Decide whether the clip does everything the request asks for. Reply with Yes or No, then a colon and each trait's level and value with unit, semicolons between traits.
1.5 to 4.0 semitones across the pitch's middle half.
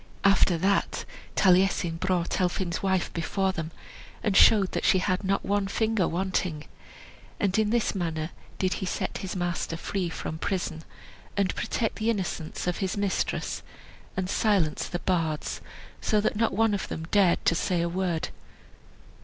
Yes: narrow, 2.5 semitones